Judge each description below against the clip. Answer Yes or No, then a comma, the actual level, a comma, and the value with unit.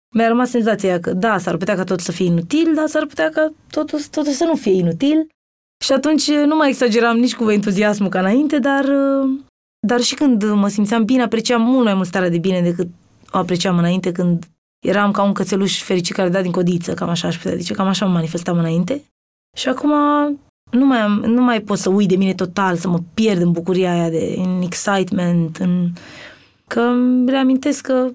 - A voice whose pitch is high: Yes, high, 210 Hz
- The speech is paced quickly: Yes, fast, 210 wpm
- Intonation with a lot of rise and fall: Yes, wide, 6.2 semitones